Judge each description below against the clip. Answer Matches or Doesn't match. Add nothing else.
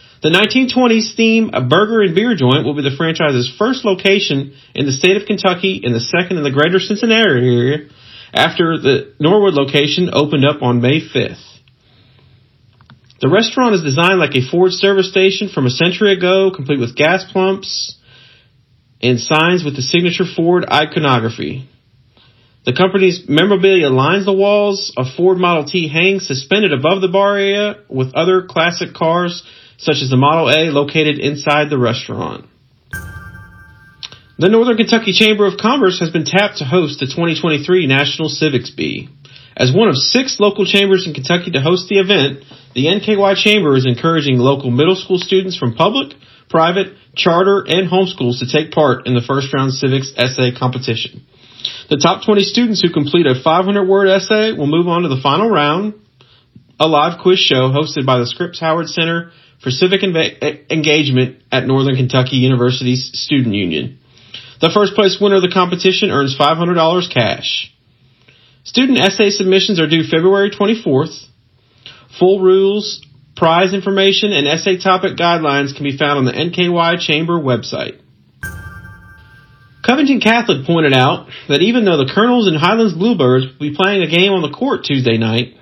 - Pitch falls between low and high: Matches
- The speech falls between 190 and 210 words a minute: Doesn't match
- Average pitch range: Doesn't match